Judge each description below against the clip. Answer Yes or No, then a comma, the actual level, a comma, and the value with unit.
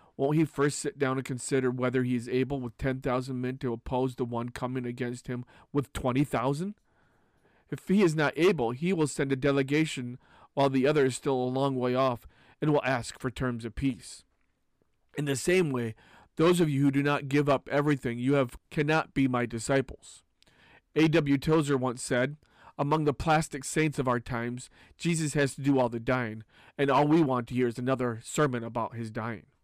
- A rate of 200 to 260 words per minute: Yes, fast, 205 wpm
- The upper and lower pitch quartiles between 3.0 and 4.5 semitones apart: No, narrow, 2.6 semitones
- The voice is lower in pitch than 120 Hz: No, low, 135 Hz